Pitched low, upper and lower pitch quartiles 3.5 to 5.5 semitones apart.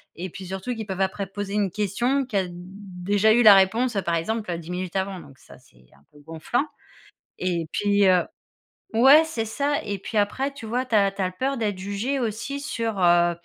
No: high, 200 Hz; average, 4.1 semitones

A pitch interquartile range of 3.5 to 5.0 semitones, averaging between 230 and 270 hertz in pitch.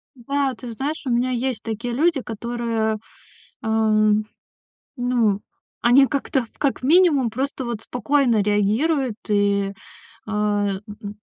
Yes: average, 3.8 semitones; high, 235 Hz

